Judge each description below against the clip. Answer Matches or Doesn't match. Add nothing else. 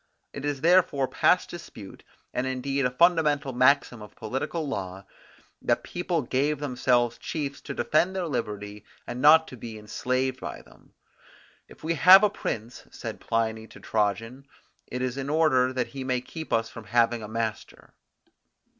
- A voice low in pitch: Matches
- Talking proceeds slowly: Doesn't match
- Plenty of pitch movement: Doesn't match